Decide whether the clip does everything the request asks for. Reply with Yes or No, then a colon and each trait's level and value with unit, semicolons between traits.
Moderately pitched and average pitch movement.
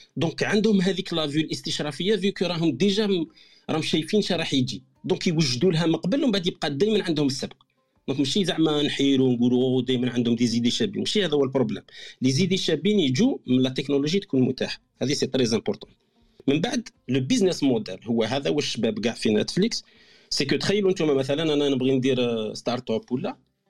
No: medium, 155 Hz; wide, 6.5 semitones